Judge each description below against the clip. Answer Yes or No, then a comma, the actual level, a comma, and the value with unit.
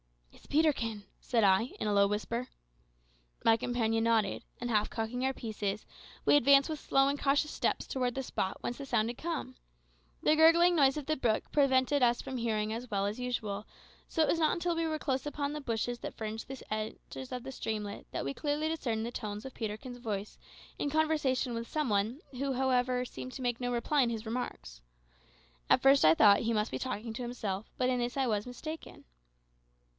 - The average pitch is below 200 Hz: No, high, 245 Hz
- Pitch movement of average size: Yes, average, 3.9 semitones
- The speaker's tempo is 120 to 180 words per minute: No, fast, 205 wpm